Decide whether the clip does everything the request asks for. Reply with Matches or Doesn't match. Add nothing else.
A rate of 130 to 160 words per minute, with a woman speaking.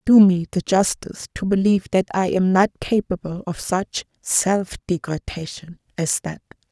Matches